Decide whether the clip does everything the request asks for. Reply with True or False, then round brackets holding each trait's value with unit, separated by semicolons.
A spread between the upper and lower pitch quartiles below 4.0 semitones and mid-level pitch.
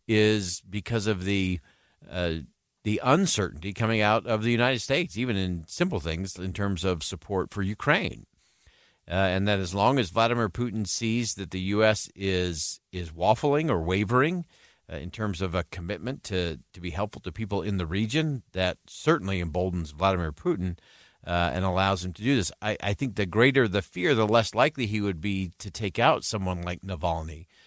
False (3.6 semitones; 100 Hz)